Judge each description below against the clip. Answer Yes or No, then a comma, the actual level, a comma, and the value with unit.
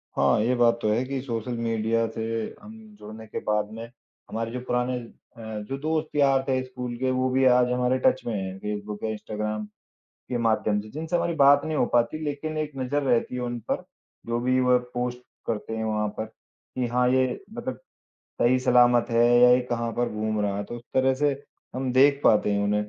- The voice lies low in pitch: Yes, low, 125 Hz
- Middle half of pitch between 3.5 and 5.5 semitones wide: No, average, 2.8 semitones